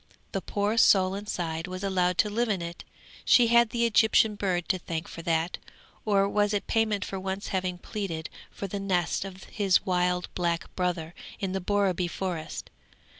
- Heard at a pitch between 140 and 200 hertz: Yes, high, 190 Hz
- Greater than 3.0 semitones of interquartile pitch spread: No, narrow, 2.4 semitones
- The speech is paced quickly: No, average, 175 wpm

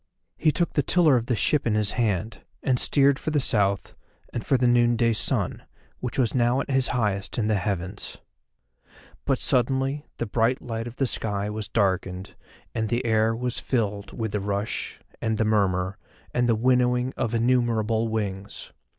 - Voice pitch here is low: Yes, low, 115 Hz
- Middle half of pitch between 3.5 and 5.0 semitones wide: No, average, 3.1 semitones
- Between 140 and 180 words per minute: Yes, average, 175 wpm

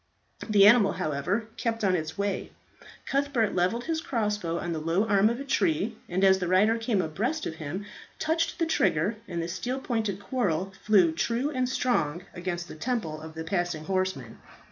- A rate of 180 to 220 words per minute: Yes, average, 185 wpm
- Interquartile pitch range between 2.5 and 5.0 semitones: No, wide, 5.4 semitones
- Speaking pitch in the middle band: No, high, 195 Hz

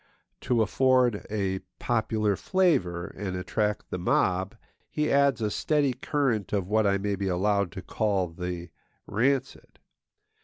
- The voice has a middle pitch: No, low, 105 Hz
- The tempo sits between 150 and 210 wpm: No, average, 140 wpm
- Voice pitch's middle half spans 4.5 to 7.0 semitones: Yes, average, 5.0 semitones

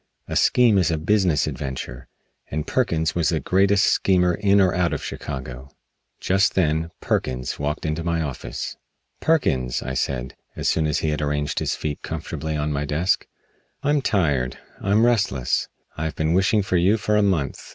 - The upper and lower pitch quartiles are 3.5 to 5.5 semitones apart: Yes, average, 4.9 semitones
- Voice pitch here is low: Yes, very low, 80 Hz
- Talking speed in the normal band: Yes, average, 175 wpm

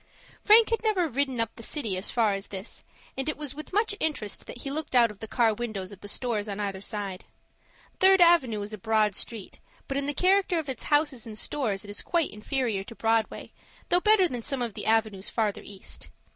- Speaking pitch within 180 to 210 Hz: No, high, 235 Hz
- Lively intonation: Yes, wide, 6.2 semitones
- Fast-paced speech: Yes, fast, 225 wpm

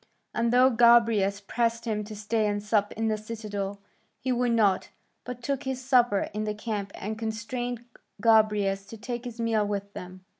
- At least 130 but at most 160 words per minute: No, average, 180 wpm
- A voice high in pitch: Yes, high, 220 Hz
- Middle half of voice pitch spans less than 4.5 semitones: Yes, narrow, 2.5 semitones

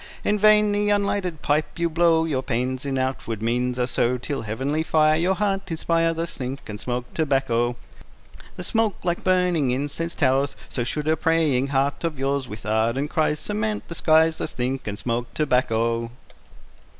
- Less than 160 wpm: No, average, 175 wpm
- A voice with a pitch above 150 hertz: No, medium, 145 Hz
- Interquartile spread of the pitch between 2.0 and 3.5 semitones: No, average, 5.1 semitones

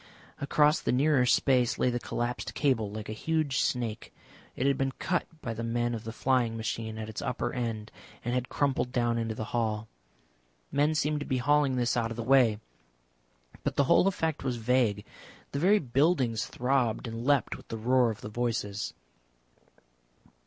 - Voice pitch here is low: Yes, low, 120 Hz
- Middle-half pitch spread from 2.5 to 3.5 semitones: Yes, average, 3.2 semitones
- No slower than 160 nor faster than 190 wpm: Yes, average, 180 wpm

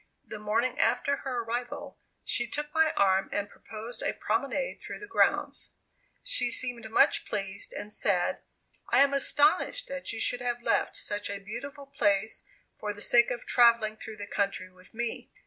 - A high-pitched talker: Yes, high, 235 Hz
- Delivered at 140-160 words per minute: No, average, 170 wpm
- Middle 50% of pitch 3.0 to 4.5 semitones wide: No, average, 5.0 semitones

